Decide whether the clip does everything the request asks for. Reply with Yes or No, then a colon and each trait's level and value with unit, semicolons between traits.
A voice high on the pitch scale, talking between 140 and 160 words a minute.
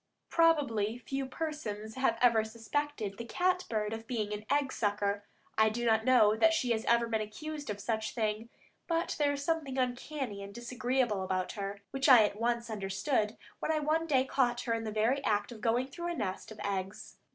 No: high, 235 Hz; fast, 205 wpm